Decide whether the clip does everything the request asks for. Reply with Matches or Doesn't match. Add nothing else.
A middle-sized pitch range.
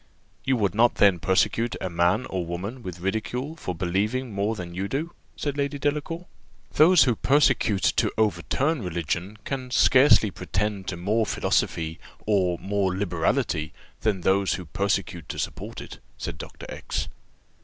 Doesn't match